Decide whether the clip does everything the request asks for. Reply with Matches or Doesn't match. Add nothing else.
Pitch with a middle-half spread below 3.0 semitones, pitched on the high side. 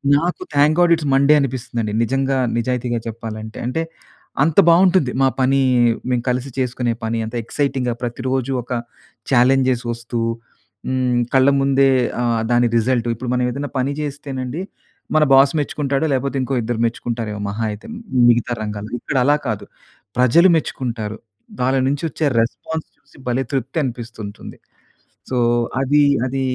Doesn't match